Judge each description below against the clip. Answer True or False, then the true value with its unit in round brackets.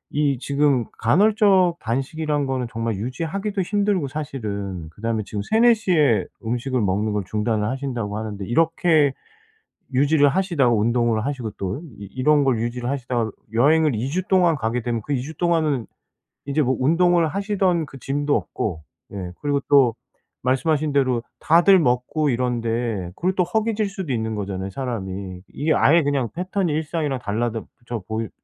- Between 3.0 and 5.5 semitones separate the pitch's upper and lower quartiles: False (5.9 semitones)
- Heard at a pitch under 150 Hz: True (135 Hz)